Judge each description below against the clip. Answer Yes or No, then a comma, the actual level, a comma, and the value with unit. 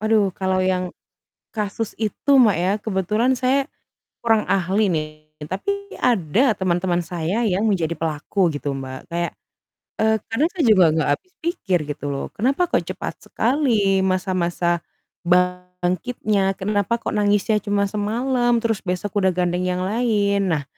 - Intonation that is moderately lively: Yes, average, 3.7 semitones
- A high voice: Yes, high, 195 Hz